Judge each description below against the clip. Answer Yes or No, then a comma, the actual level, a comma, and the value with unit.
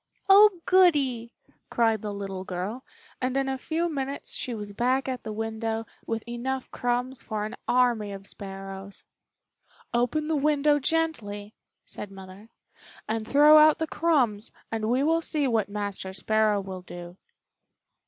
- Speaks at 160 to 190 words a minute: No, average, 150 wpm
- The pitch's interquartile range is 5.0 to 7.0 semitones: Yes, average, 5.3 semitones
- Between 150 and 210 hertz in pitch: No, high, 235 Hz